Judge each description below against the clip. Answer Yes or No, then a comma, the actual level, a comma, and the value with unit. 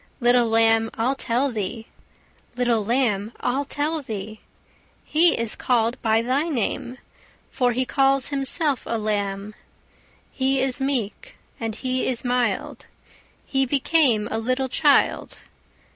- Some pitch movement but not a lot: Yes, average, 3.3 semitones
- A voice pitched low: No, high, 245 Hz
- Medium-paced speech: No, slow, 130 wpm